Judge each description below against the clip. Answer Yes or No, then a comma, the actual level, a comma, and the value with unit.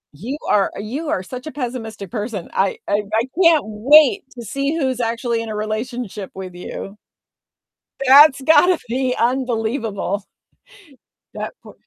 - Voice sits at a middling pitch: No, high, 235 Hz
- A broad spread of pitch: No, average, 4.1 semitones